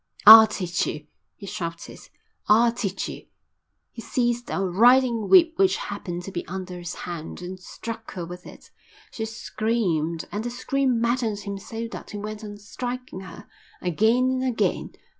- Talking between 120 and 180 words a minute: Yes, average, 165 wpm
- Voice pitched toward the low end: No, high, 215 Hz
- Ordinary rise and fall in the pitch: Yes, average, 4.7 semitones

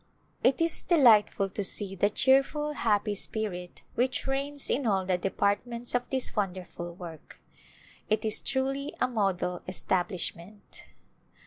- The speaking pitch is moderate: No, high, 210 Hz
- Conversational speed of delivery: No, slow, 130 wpm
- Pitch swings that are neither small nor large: No, wide, 5.8 semitones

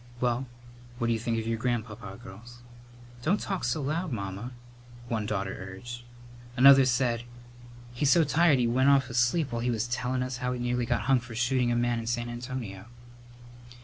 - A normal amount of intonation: No, narrow, 1.9 semitones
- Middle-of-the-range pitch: No, low, 120 Hz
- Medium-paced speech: Yes, average, 180 wpm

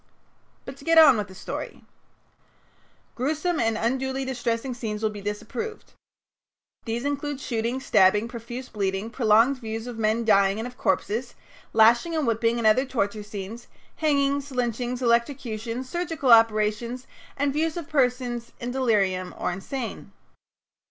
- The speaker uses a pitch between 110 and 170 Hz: No, high, 235 Hz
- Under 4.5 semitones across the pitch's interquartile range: Yes, average, 3.5 semitones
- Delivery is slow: No, average, 145 wpm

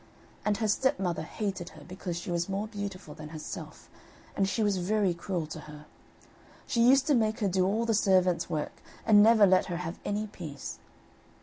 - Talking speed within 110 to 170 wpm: No, average, 190 wpm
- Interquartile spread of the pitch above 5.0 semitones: No, average, 3.6 semitones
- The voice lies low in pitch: No, high, 195 Hz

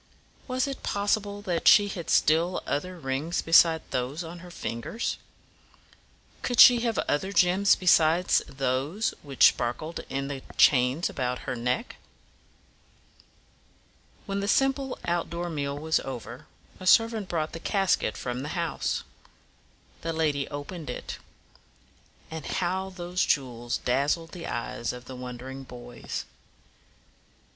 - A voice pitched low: No, medium, 160 Hz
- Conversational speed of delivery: No, slow, 130 wpm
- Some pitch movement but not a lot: No, wide, 5.7 semitones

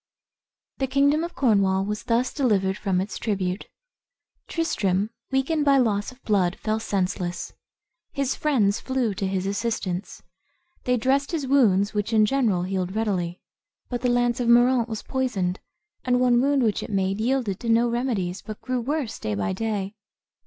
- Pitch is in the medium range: No, high, 225 Hz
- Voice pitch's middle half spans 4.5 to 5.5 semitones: Yes, average, 4.8 semitones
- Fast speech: No, average, 165 wpm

